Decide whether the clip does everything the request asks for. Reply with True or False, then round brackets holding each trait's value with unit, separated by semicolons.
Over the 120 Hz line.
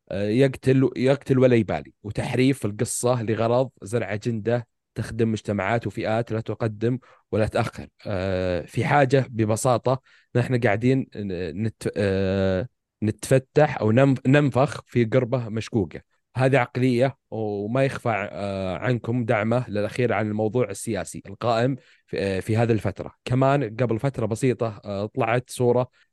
False (115 Hz)